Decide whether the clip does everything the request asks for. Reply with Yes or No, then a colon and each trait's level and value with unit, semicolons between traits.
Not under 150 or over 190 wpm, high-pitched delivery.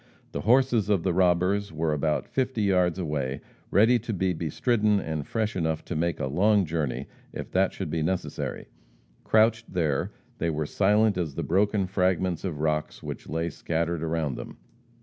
No: average, 170 wpm; very low, 90 Hz